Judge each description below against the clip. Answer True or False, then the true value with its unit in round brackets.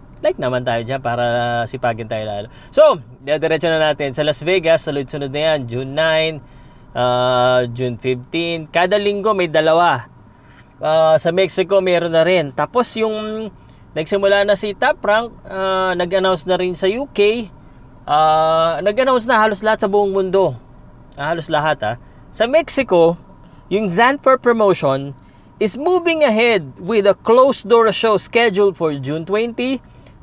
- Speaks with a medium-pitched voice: True (170 Hz)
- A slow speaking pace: False (150 wpm)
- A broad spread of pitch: True (7.1 semitones)